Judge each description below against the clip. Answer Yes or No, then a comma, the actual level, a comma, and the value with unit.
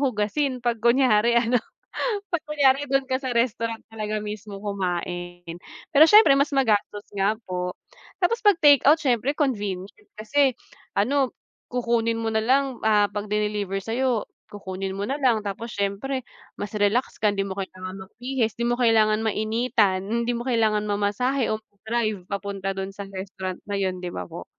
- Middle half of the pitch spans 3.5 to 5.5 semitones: Yes, average, 4.2 semitones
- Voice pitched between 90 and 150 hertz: No, high, 220 Hz